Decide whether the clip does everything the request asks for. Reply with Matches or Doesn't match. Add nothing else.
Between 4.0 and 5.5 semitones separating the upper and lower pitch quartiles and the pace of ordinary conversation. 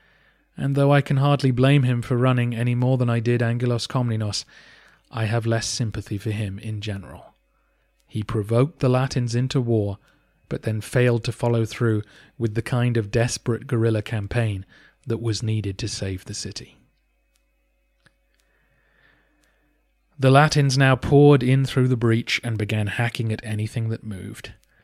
Doesn't match